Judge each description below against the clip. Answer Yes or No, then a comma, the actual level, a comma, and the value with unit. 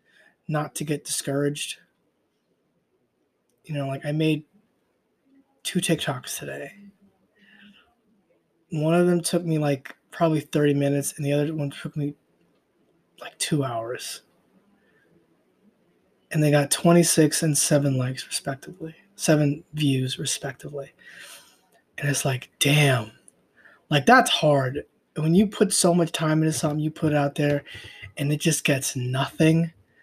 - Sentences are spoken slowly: Yes, slow, 130 wpm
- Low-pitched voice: No, medium, 150 Hz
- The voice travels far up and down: No, average, 3.0 semitones